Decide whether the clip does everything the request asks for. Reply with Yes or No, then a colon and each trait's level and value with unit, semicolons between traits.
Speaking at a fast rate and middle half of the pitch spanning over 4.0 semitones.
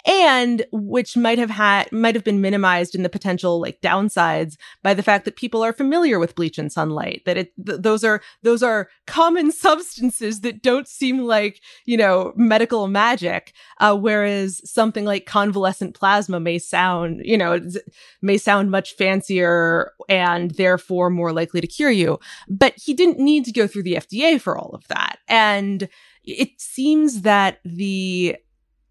No: average, 170 wpm; average, 4.4 semitones